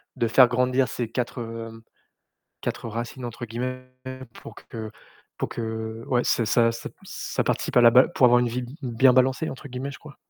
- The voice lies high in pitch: No, low, 120 Hz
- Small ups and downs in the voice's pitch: Yes, narrow, 1.8 semitones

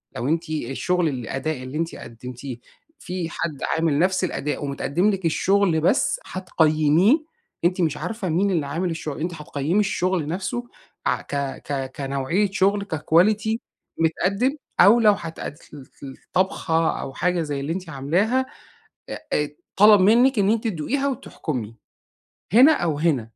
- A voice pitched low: No, medium, 170 Hz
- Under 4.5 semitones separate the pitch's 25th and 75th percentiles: No, average, 5.1 semitones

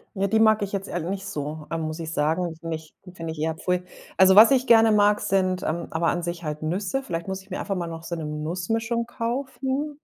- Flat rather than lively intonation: No, average, 4.8 semitones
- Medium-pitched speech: Yes, medium, 180 Hz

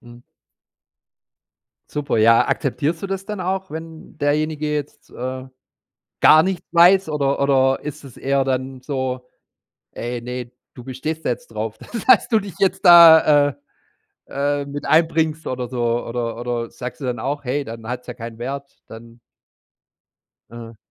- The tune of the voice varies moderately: Yes, average, 4.4 semitones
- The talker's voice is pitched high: No, medium, 140 Hz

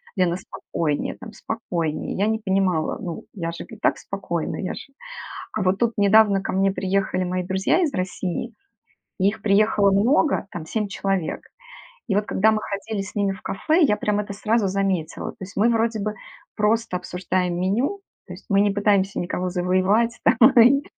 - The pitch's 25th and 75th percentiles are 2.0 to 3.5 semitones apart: Yes, average, 2.8 semitones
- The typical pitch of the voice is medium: No, high, 195 Hz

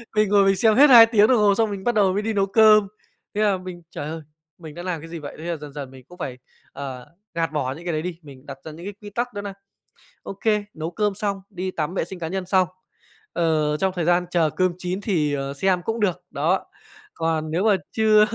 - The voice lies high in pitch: No, medium, 180 Hz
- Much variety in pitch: No, average, 4.5 semitones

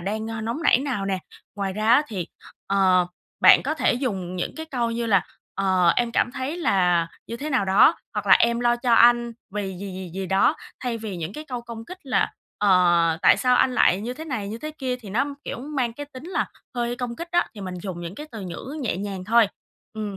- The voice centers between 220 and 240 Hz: Yes, high, 225 Hz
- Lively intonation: No, average, 4.6 semitones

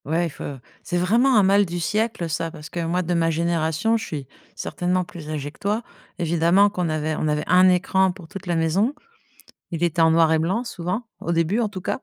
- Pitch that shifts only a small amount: No, average, 3.1 semitones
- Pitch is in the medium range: Yes, medium, 175 Hz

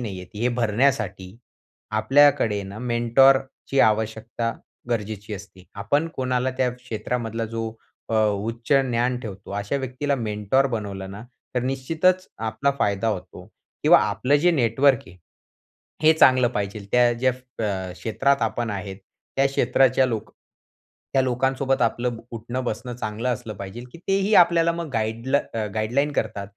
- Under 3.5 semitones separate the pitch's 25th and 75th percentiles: No, average, 3.8 semitones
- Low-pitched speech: Yes, low, 120 Hz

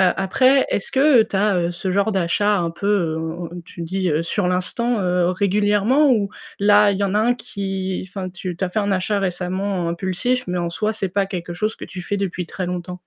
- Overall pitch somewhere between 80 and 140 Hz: No, high, 190 Hz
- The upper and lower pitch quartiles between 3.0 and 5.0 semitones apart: No, narrow, 2.6 semitones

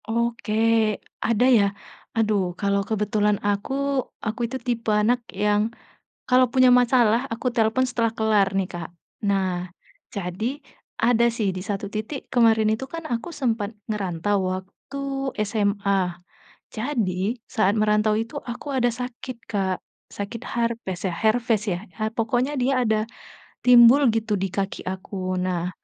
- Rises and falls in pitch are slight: No, average, 3.2 semitones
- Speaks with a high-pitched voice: Yes, high, 220 Hz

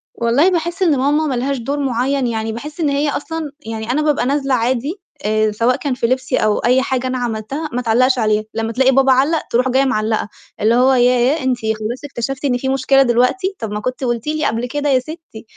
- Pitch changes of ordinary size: Yes, average, 3.3 semitones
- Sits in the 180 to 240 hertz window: No, very high, 255 Hz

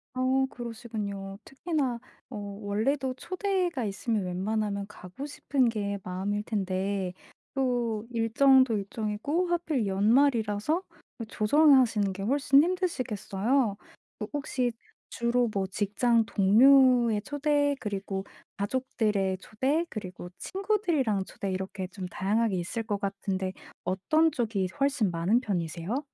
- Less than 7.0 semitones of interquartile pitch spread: Yes, average, 5.1 semitones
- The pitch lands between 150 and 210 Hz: No, high, 220 Hz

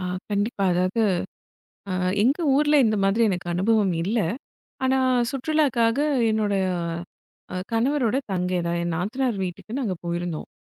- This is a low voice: No, high, 215 Hz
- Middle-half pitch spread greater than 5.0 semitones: Yes, wide, 5.5 semitones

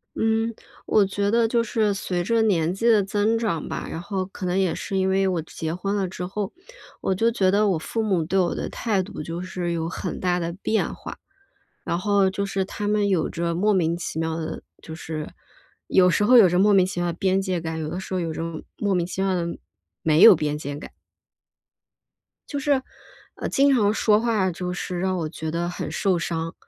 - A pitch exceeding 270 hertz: No, high, 190 Hz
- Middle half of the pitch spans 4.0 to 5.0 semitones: No, average, 3.2 semitones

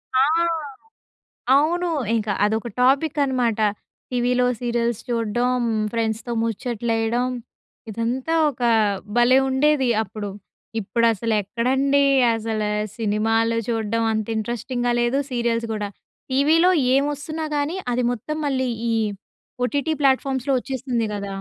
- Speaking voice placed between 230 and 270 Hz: Yes, high, 240 Hz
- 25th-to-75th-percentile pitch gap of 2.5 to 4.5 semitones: Yes, average, 2.9 semitones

